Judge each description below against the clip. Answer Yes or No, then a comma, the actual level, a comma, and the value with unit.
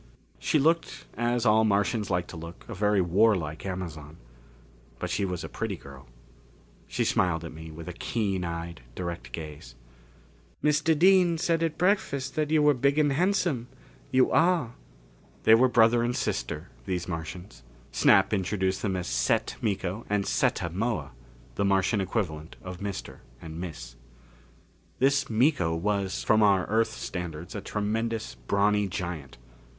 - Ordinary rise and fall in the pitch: No, wide, 5.9 semitones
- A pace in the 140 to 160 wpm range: Yes, average, 150 wpm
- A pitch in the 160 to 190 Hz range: No, low, 100 Hz